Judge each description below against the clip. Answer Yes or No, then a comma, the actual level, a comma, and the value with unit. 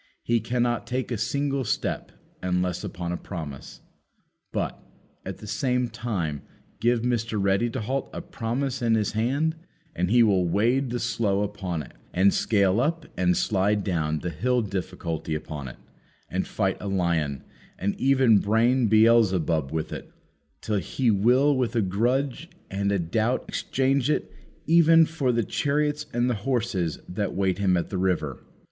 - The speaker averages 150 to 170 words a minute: Yes, average, 165 wpm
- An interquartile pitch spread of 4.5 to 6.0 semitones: Yes, average, 5.3 semitones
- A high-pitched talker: No, low, 110 Hz